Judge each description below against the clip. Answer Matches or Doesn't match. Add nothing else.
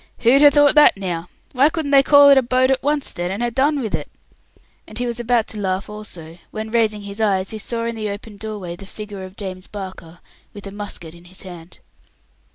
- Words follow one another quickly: Matches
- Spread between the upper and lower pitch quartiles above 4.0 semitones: Matches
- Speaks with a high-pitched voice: Matches